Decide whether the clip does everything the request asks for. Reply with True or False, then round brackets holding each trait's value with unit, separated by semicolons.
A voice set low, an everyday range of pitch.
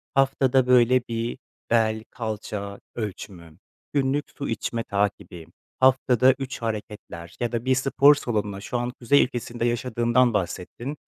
True (120 Hz; 3.6 semitones)